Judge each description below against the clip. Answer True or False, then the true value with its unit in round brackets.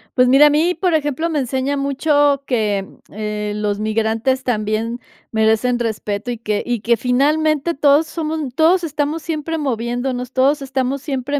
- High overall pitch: True (260 Hz)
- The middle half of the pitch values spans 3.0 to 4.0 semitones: False (4.6 semitones)